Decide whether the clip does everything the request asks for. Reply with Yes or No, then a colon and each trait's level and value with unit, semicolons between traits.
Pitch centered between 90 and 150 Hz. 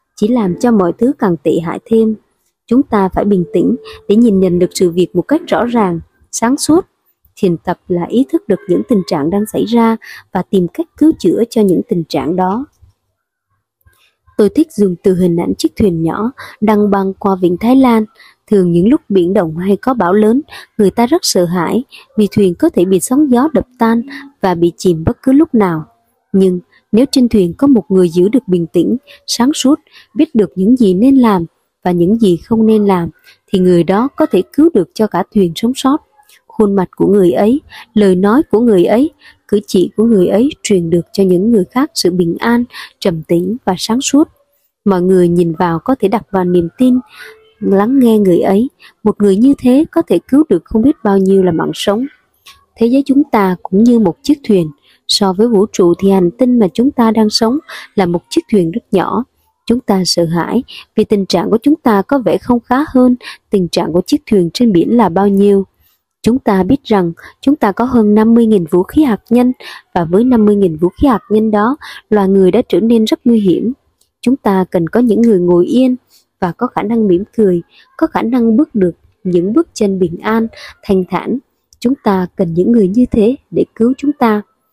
No: high, 215 Hz